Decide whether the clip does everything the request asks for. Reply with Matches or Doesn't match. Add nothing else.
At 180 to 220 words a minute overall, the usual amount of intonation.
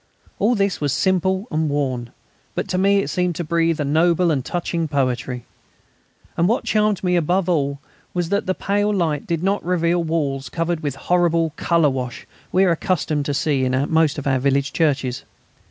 Matches